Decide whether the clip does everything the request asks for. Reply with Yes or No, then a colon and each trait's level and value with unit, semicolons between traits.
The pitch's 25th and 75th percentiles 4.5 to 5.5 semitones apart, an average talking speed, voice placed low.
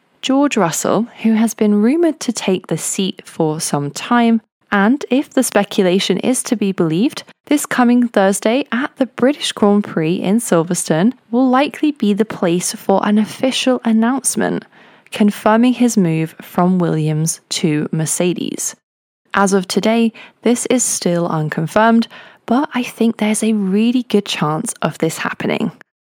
No: average, 5.2 semitones; average, 150 wpm; high, 215 Hz